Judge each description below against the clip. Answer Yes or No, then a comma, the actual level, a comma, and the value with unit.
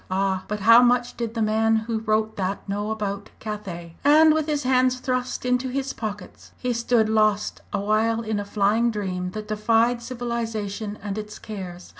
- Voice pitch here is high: Yes, high, 220 Hz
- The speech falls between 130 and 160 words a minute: No, average, 175 wpm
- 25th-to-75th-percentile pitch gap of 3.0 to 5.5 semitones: No, narrow, 2.6 semitones